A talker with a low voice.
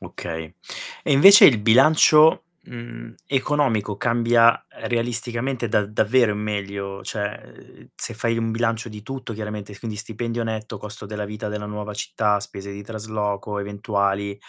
Yes: low, 110 Hz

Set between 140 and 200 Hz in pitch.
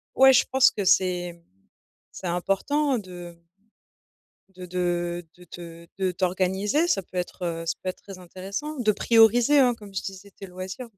Yes: medium, 185 Hz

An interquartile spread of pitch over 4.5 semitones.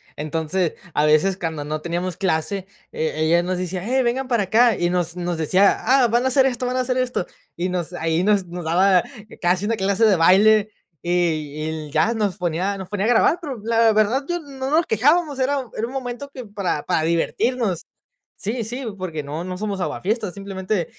Yes: wide, 5.5 semitones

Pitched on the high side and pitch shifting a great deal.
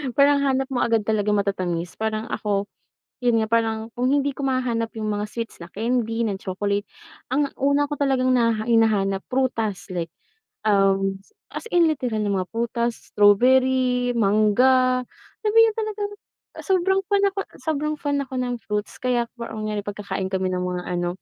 No: high, 230 Hz; average, 4.2 semitones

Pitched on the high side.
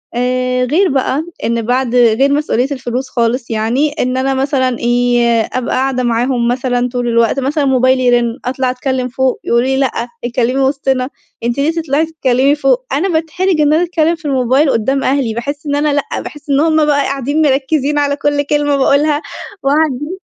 Yes: very high, 265 Hz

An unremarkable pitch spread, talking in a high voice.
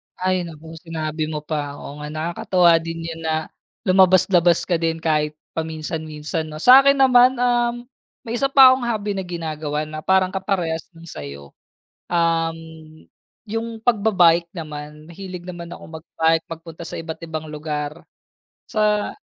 No: average, 3.4 semitones; medium, 165 Hz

